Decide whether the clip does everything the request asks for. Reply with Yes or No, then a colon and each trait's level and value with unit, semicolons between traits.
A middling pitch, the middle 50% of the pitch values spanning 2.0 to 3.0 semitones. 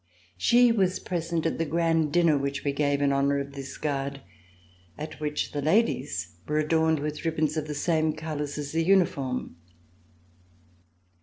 Yes: medium, 150 Hz; narrow, 2.5 semitones